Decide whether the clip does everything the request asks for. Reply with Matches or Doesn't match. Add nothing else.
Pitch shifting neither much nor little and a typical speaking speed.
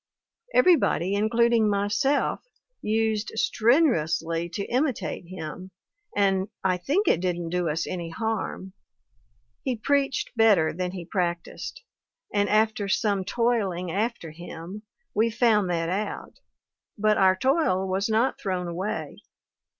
Doesn't match